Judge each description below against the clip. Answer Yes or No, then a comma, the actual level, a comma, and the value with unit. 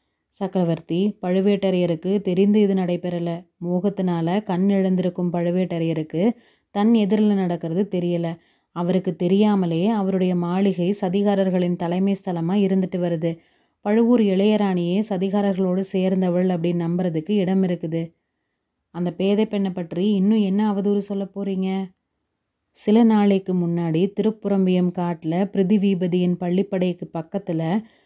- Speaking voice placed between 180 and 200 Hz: Yes, high, 190 Hz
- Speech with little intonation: Yes, narrow, 2.3 semitones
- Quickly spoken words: No, average, 100 wpm